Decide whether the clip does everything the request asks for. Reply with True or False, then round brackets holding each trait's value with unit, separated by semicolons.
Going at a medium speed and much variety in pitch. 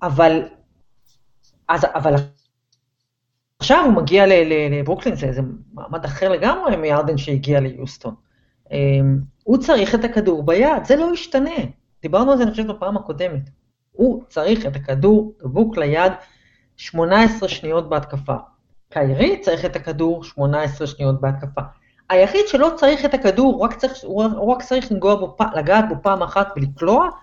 True (135 wpm; 7.7 semitones)